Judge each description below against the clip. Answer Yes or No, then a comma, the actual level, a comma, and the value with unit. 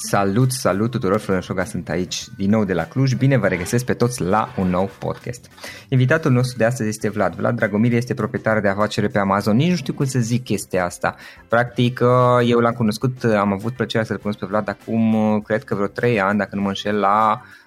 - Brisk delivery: Yes, fast, 220 wpm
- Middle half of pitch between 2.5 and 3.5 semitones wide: Yes, average, 3.1 semitones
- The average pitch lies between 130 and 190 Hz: No, low, 110 Hz